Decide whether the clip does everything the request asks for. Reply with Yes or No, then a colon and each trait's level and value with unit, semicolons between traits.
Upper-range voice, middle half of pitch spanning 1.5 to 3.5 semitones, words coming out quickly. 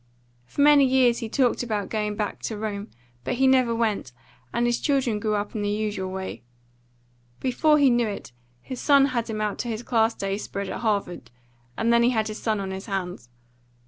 Yes: high, 220 Hz; average, 3.1 semitones; fast, 210 wpm